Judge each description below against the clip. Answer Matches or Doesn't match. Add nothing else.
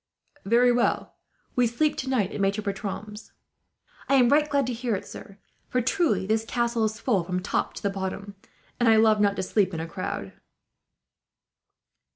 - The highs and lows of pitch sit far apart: Doesn't match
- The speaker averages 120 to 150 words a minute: Doesn't match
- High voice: Matches